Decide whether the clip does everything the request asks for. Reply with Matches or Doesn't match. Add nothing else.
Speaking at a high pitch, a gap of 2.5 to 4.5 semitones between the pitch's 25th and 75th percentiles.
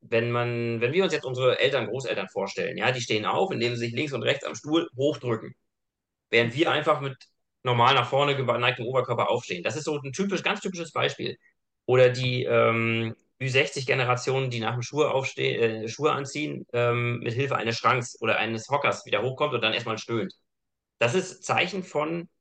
Doesn't match